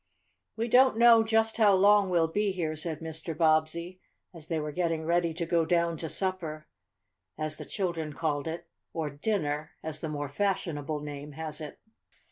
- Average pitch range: Yes, average, 3.3 semitones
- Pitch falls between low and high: Yes, medium, 165 Hz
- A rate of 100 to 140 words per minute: No, average, 175 wpm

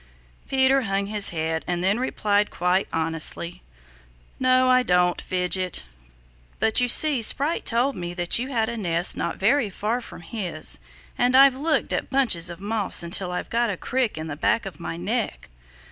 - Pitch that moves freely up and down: Yes, wide, 6.1 semitones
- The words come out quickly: No, average, 175 wpm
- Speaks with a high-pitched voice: Yes, high, 205 Hz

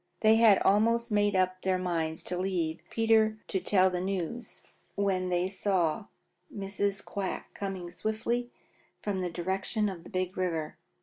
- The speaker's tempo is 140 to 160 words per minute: Yes, average, 150 wpm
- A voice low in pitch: No, high, 190 Hz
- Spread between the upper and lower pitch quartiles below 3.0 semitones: Yes, narrow, 2.5 semitones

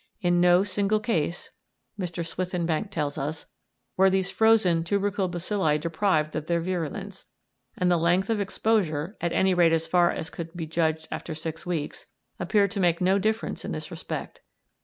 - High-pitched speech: No, medium, 175 Hz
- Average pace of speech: Yes, average, 170 wpm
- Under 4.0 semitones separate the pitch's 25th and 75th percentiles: Yes, average, 3.1 semitones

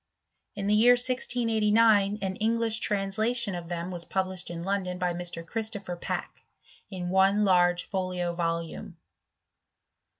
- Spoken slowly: Yes, slow, 130 wpm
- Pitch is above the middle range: Yes, high, 195 Hz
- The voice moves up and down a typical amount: Yes, average, 3.5 semitones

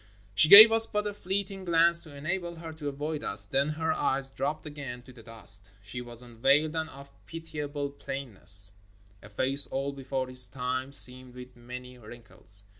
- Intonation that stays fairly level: No, average, 4.2 semitones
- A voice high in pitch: No, medium, 140 Hz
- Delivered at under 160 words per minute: No, average, 180 wpm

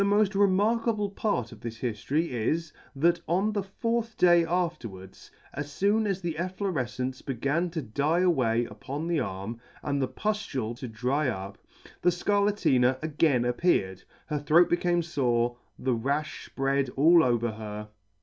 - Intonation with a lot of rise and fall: Yes, wide, 6.7 semitones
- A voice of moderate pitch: Yes, medium, 150 Hz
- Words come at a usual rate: Yes, average, 160 wpm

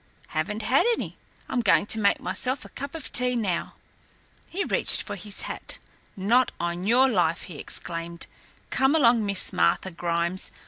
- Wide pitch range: Yes, wide, 6.5 semitones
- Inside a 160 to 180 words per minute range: Yes, average, 165 wpm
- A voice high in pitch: Yes, high, 205 Hz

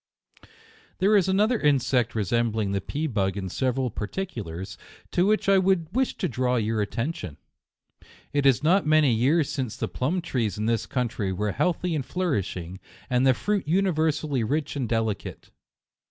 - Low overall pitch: Yes, low, 130 Hz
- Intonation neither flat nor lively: No, wide, 7.3 semitones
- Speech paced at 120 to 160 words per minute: No, average, 170 wpm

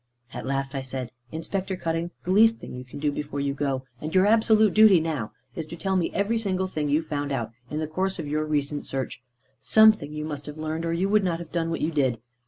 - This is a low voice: No, medium, 155 Hz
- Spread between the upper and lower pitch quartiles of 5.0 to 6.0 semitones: No, average, 4.6 semitones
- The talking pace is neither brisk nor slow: No, fast, 245 wpm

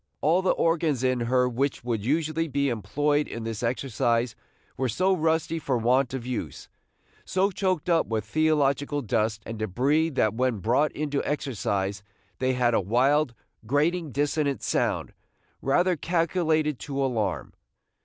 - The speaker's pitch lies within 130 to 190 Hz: Yes, low, 135 Hz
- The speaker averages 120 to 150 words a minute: Yes, average, 145 wpm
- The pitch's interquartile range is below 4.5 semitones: No, average, 4.8 semitones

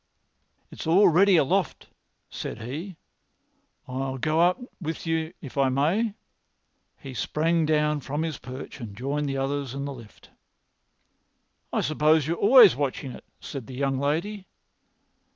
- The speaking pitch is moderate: Yes, medium, 150 Hz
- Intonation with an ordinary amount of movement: Yes, average, 3.5 semitones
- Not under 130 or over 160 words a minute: Yes, average, 150 wpm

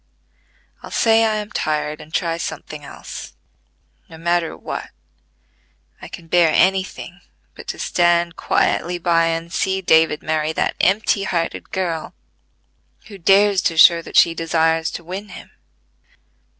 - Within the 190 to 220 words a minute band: No, average, 145 wpm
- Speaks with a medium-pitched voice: Yes, medium, 170 Hz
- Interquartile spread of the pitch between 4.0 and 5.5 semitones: No, average, 2.7 semitones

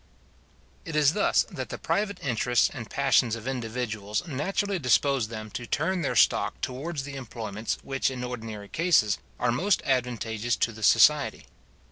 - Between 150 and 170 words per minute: Yes, average, 155 wpm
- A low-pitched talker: Yes, low, 125 Hz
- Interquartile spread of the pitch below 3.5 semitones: No, average, 4.4 semitones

